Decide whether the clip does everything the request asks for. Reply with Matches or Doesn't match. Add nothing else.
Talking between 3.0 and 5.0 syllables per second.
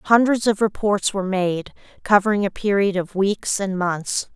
Matches